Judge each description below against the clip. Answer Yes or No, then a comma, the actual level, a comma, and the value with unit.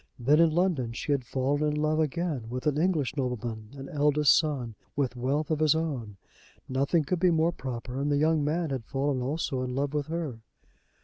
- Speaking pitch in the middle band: Yes, medium, 145 Hz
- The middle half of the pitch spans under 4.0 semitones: Yes, average, 3.3 semitones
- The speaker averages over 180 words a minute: Yes, average, 200 wpm